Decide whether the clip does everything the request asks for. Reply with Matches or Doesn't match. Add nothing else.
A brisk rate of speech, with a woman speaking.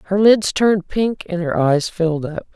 Matches